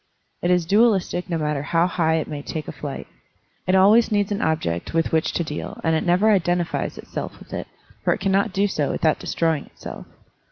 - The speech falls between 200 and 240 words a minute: Yes, fast, 205 wpm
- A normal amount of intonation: Yes, average, 3.4 semitones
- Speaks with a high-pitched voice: No, medium, 170 Hz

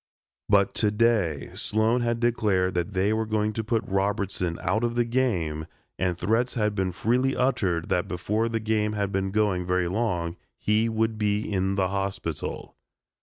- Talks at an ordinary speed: Yes, average, 170 wpm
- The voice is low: Yes, low, 105 Hz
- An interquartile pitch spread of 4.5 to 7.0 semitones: No, average, 3.3 semitones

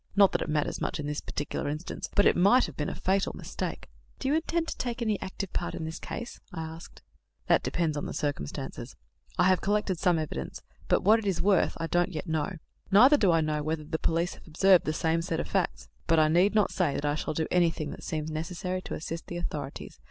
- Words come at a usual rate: No, fast, 235 wpm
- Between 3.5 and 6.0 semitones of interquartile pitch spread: Yes, average, 3.8 semitones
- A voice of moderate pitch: Yes, medium, 170 Hz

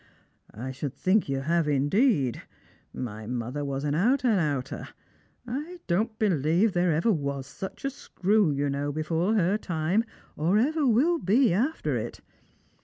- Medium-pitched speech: Yes, medium, 170 Hz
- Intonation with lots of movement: Yes, wide, 7.5 semitones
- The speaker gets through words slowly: No, average, 160 wpm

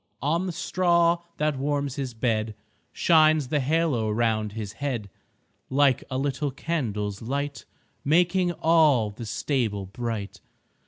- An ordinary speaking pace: No, slow, 125 wpm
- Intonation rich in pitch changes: Yes, wide, 5.8 semitones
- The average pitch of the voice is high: No, low, 135 Hz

